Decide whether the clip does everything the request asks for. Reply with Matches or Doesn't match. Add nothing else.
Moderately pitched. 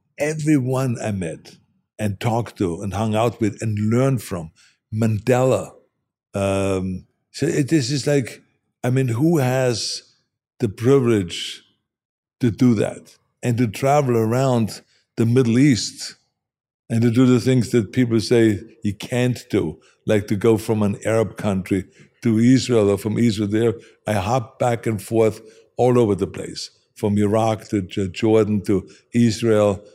Doesn't match